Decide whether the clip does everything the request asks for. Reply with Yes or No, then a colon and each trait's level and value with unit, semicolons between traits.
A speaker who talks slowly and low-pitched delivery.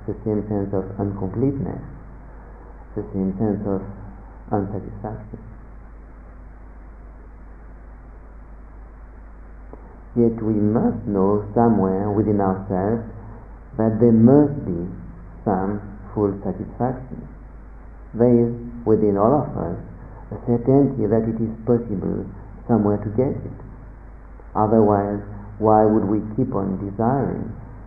Yes: slow, 100 wpm; low, 105 Hz